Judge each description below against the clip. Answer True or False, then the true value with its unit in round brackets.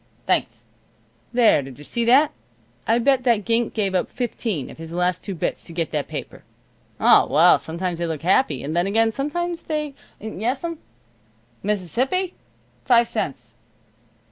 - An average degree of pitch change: False (6.9 semitones)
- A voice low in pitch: False (215 Hz)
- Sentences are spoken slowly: False (155 wpm)